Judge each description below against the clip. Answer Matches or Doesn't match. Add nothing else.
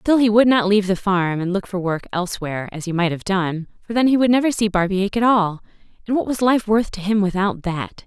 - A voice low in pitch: Doesn't match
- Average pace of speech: Doesn't match